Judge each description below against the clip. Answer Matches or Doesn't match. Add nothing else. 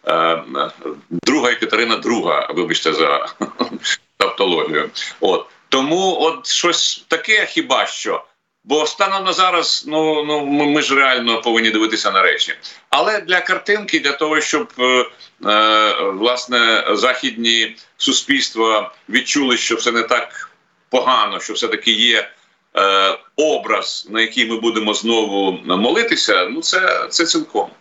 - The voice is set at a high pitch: Doesn't match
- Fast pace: Doesn't match